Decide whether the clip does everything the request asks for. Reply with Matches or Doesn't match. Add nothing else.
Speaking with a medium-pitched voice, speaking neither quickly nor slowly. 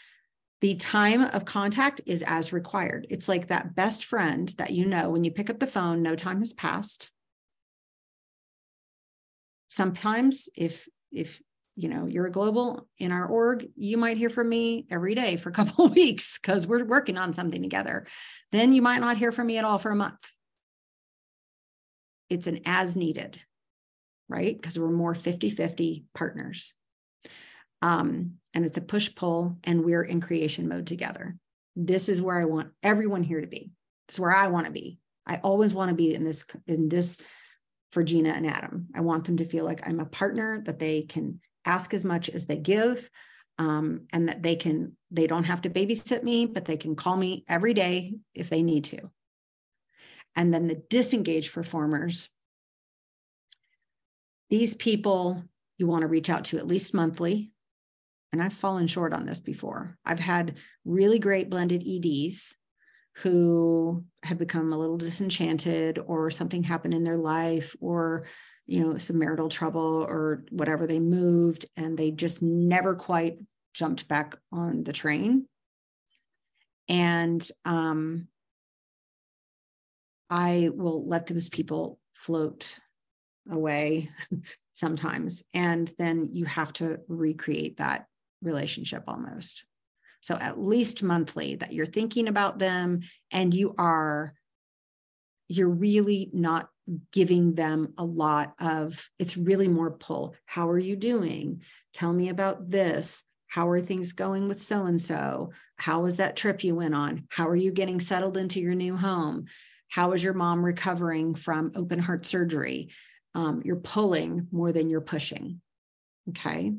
Matches